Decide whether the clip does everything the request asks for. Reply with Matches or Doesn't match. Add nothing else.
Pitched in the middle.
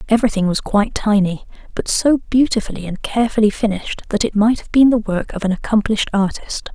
Doesn't match